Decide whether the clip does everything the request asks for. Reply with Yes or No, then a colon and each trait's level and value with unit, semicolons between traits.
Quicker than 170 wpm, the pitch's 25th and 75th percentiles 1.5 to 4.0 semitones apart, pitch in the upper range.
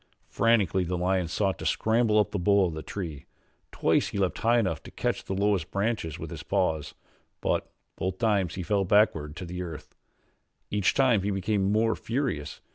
No: average, 190 wpm; average, 3.3 semitones; very low, 95 Hz